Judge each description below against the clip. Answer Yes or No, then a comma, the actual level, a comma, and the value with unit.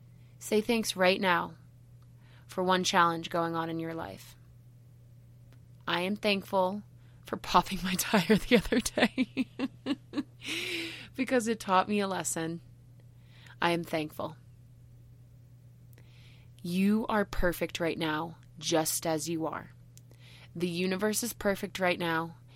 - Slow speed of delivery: Yes, slow, 120 wpm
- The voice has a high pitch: No, medium, 165 Hz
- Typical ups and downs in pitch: No, wide, 7.6 semitones